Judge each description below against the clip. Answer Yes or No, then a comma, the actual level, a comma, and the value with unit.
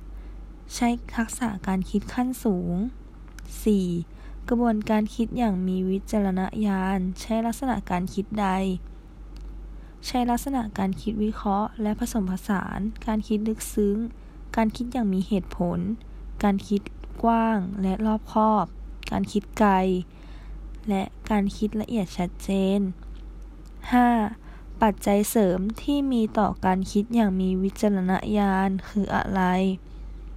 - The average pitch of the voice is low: No, high, 205 Hz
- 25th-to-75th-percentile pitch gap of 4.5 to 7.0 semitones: No, average, 2.8 semitones